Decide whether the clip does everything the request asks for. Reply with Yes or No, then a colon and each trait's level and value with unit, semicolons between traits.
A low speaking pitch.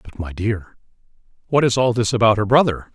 Yes: low, 115 Hz